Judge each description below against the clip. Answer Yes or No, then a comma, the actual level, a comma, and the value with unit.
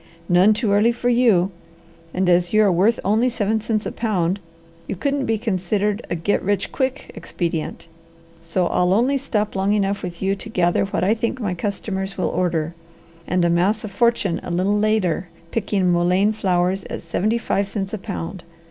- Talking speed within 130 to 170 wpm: No, average, 185 wpm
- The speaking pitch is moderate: No, high, 195 Hz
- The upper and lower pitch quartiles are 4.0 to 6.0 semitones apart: No, average, 3.3 semitones